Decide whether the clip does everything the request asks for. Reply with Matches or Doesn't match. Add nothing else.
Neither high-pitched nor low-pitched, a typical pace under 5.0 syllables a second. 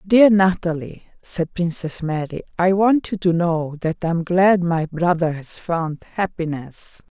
Matches